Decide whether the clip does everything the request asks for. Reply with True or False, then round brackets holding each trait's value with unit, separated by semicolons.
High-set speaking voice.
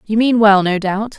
True (210 Hz)